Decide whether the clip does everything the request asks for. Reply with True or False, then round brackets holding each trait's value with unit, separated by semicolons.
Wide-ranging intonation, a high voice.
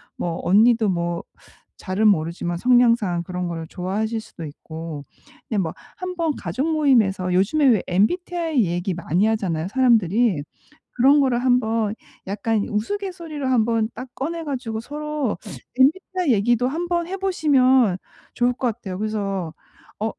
True (6.6 semitones; 225 Hz)